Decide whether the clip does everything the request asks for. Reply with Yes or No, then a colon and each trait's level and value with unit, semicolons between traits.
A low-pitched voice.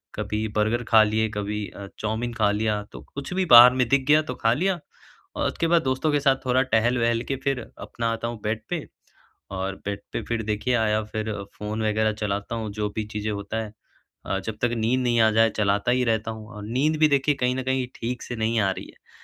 Yes: low, 115 Hz